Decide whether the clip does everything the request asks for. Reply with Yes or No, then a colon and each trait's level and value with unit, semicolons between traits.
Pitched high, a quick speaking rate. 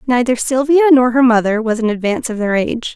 Yes: high, 240 Hz; fast, 225 wpm